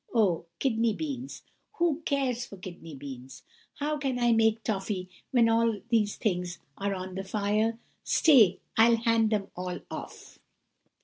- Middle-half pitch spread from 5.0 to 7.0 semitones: No, average, 4.0 semitones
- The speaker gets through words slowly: No, average, 145 wpm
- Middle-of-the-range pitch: No, high, 220 Hz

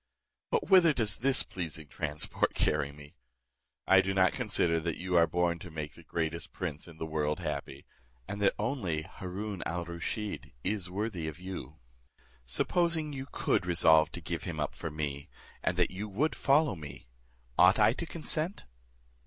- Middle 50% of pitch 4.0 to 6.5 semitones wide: Yes, average, 5.3 semitones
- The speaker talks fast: No, average, 170 wpm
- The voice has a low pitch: Yes, very low, 90 Hz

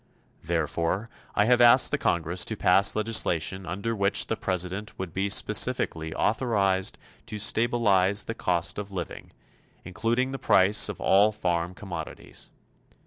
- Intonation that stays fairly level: No, average, 3.3 semitones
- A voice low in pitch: Yes, low, 100 Hz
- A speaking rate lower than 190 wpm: Yes, average, 140 wpm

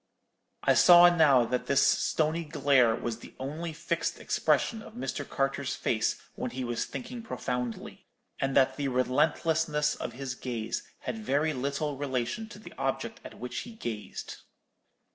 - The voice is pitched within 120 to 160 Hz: Yes, medium, 140 Hz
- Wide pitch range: No, average, 4.2 semitones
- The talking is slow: No, average, 155 wpm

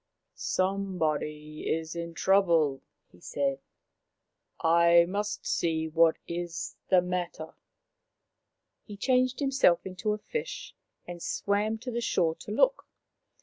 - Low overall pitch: No, medium, 180 Hz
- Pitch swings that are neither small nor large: Yes, average, 4.3 semitones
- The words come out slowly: Yes, slow, 125 wpm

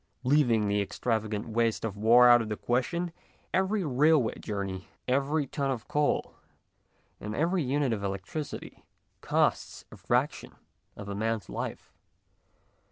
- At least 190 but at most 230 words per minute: No, average, 140 wpm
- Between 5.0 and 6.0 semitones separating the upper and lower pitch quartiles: Yes, wide, 5.4 semitones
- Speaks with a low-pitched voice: Yes, low, 120 Hz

